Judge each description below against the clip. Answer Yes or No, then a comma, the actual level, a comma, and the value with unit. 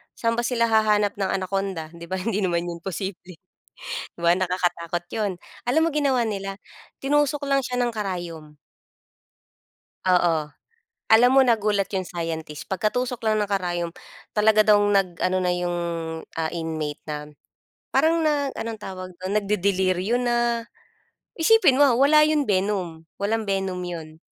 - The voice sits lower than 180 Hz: No, high, 195 Hz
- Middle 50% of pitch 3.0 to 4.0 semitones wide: No, average, 4.7 semitones